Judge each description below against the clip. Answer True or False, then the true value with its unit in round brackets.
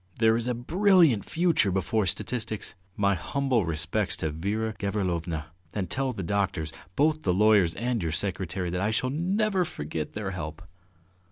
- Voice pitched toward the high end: False (105 Hz)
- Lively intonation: True (6.0 semitones)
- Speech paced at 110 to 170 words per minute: True (160 wpm)